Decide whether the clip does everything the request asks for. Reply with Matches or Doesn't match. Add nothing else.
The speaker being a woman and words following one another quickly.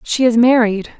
Doesn't match